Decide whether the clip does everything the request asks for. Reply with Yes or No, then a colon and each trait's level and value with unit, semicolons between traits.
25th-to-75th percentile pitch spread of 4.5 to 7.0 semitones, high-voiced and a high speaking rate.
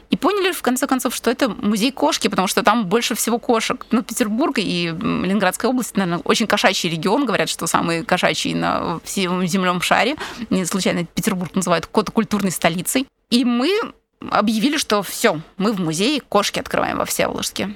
Yes: average, 4.8 semitones; high, 215 Hz; fast, 180 wpm